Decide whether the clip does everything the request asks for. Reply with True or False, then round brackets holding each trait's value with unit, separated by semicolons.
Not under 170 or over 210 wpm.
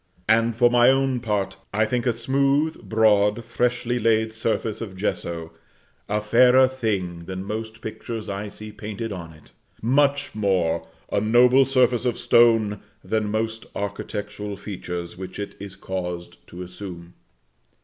False (145 wpm)